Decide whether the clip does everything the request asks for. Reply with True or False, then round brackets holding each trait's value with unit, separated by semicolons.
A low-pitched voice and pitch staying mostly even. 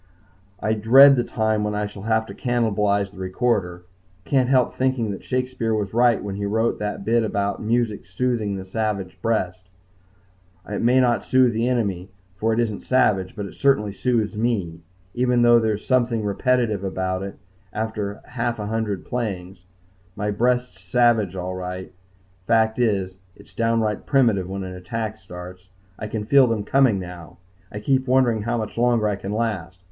False (110 Hz; 3.5 semitones)